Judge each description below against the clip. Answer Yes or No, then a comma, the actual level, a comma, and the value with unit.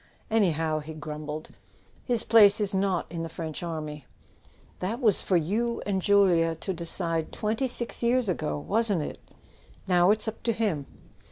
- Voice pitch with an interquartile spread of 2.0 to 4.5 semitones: No, average, 5.1 semitones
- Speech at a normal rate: Yes, average, 160 wpm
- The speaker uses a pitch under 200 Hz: Yes, medium, 185 Hz